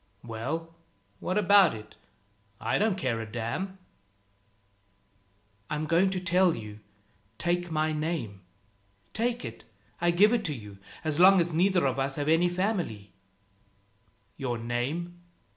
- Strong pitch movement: Yes, wide, 7.2 semitones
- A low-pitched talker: No, medium, 165 Hz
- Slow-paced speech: Yes, slow, 130 wpm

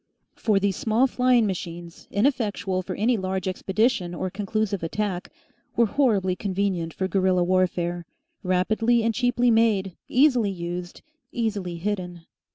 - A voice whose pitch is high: Yes, high, 195 Hz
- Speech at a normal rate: No, slow, 130 wpm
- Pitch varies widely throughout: No, average, 3.7 semitones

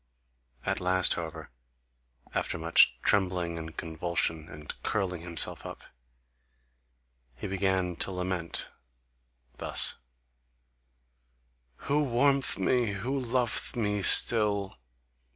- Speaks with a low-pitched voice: Yes, very low, 95 Hz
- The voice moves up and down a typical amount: Yes, average, 4.2 semitones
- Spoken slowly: Yes, slow, 95 wpm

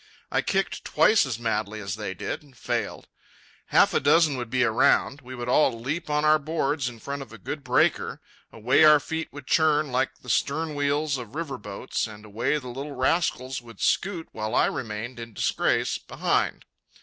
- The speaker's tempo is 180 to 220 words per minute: Yes, average, 190 wpm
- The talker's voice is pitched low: Yes, low, 130 Hz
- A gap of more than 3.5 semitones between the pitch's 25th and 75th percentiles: Yes, average, 4.4 semitones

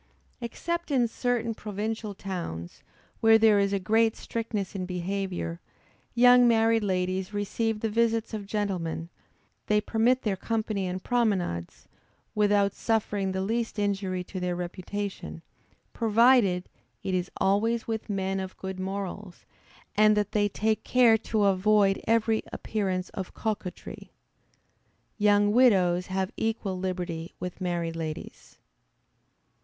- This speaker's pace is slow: Yes, slow, 130 wpm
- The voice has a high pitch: Yes, high, 205 Hz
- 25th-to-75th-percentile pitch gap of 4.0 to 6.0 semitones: No, average, 3.1 semitones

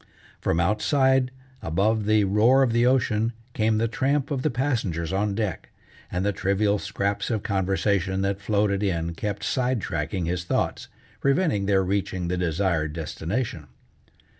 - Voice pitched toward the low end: Yes, low, 100 Hz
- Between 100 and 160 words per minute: Yes, average, 150 wpm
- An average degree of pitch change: Yes, average, 3.8 semitones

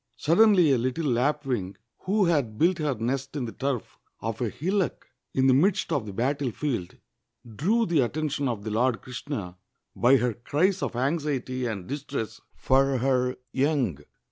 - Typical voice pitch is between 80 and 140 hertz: Yes, low, 135 Hz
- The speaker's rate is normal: Yes, average, 160 wpm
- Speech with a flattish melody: No, average, 4.0 semitones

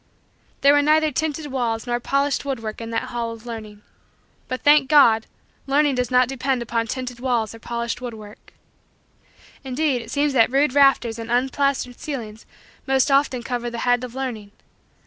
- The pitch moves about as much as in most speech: Yes, average, 3.1 semitones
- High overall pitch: Yes, very high, 250 Hz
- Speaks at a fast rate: No, average, 165 wpm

